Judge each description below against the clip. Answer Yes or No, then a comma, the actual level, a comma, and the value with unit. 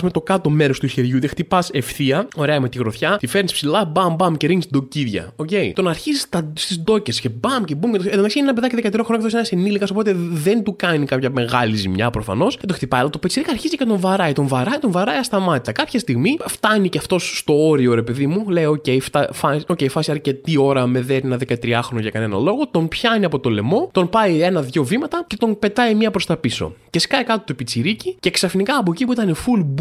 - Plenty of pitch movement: Yes, wide, 7.3 semitones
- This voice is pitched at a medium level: Yes, medium, 170 Hz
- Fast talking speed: Yes, fast, 245 wpm